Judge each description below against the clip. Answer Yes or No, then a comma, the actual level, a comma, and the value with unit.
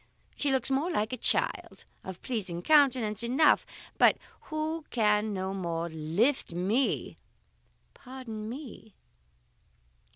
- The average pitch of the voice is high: Yes, high, 225 Hz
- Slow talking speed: Yes, slow, 120 wpm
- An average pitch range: No, wide, 5.8 semitones